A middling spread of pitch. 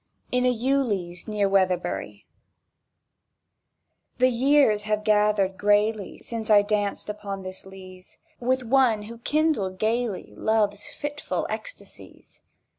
Yes: average, 3.8 semitones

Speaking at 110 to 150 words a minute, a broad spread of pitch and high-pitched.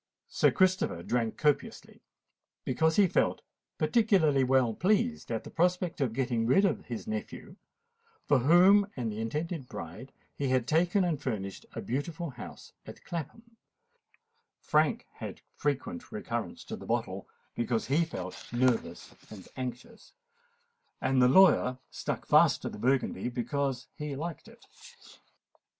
No: slow, 135 wpm; wide, 6.8 semitones; medium, 140 Hz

